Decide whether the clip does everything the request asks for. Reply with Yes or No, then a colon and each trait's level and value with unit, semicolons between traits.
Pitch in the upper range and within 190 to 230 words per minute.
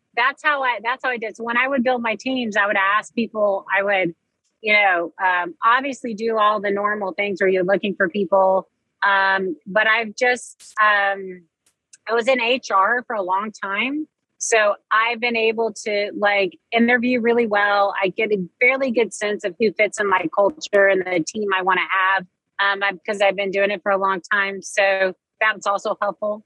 Yes: high, 205 Hz; average, 200 wpm